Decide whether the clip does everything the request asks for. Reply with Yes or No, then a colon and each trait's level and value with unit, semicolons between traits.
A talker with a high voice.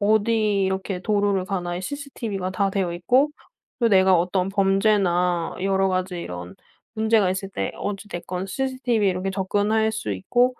Yes: high, 195 Hz